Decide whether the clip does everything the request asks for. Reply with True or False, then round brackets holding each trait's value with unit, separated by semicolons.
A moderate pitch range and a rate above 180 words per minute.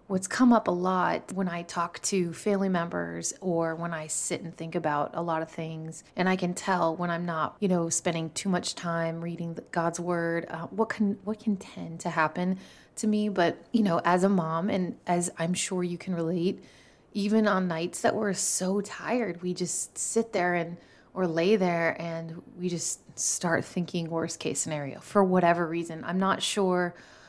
False (2.3 semitones; 200 wpm)